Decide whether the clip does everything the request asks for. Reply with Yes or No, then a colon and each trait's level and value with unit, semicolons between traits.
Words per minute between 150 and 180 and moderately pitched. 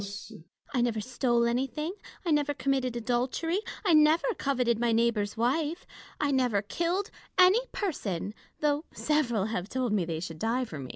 No: average, 160 wpm; very high, 255 Hz